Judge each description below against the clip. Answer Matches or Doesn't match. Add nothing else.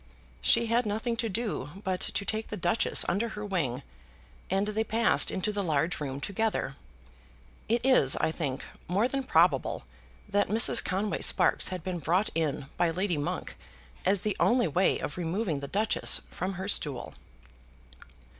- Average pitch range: Matches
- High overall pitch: Matches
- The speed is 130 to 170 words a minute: Matches